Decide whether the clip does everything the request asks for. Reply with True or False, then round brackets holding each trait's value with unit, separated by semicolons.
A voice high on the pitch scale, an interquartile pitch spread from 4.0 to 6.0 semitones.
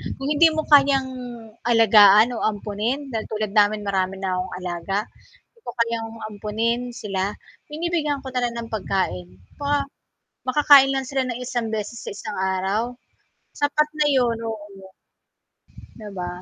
True (225 Hz; 4.8 semitones)